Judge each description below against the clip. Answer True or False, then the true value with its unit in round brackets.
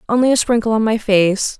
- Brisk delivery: True (225 wpm)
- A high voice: True (220 Hz)